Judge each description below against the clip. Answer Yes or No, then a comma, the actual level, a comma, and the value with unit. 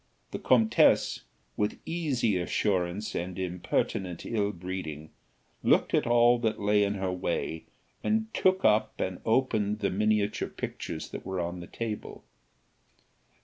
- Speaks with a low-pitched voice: Yes, low, 105 Hz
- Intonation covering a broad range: No, average, 3.7 semitones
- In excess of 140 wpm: No, slow, 135 wpm